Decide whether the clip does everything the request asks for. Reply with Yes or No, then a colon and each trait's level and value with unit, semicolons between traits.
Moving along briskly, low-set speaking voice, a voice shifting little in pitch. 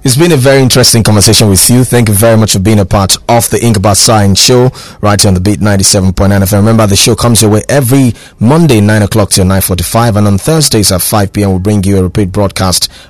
No: fast, 260 wpm; low, 105 Hz; average, 3.0 semitones